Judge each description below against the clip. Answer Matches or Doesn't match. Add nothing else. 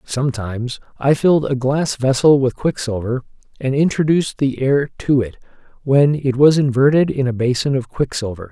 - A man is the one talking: Matches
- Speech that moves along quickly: Doesn't match